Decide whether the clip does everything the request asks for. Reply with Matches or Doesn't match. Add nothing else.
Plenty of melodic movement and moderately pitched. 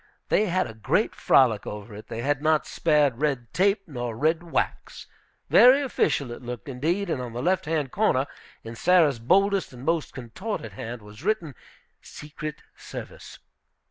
Matches